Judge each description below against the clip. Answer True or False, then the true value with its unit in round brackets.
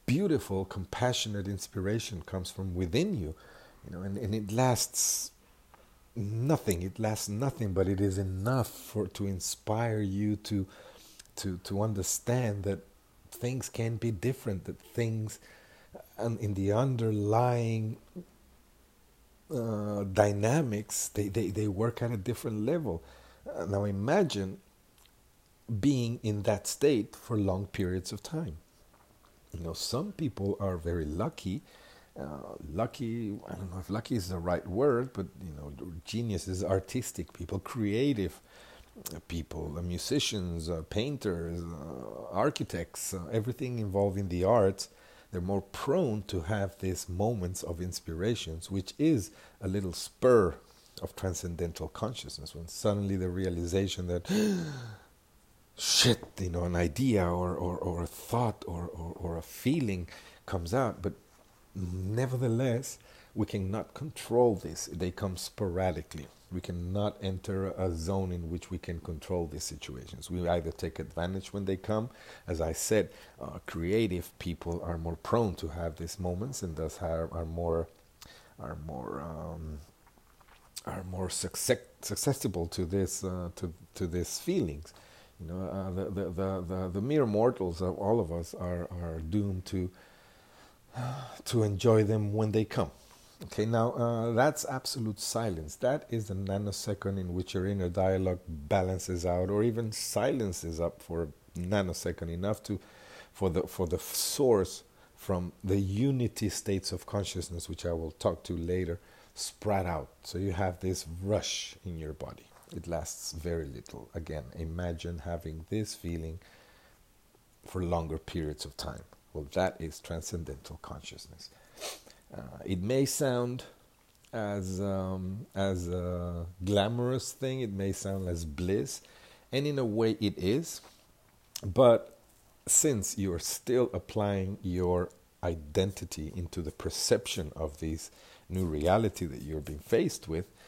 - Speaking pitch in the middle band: False (95 Hz)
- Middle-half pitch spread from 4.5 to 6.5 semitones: False (3.8 semitones)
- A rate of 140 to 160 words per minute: True (145 wpm)